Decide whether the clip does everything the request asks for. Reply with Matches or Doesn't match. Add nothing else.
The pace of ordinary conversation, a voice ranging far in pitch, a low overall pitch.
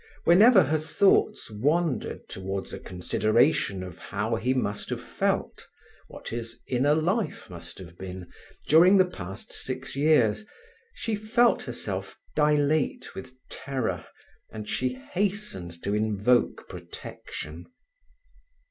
Doesn't match